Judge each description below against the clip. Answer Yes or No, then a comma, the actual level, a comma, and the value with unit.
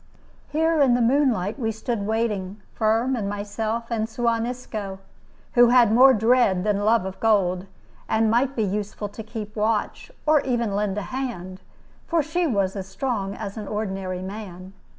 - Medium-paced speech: Yes, average, 170 wpm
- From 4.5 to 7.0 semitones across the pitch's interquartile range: No, average, 3.4 semitones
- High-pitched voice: Yes, high, 220 Hz